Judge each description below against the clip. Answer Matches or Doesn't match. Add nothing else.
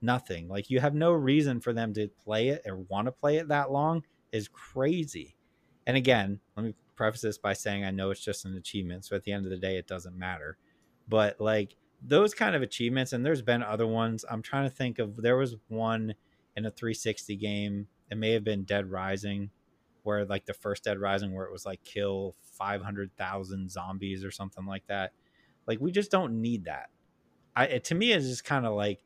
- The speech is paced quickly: Matches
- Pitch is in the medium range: Doesn't match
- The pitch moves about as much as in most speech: Matches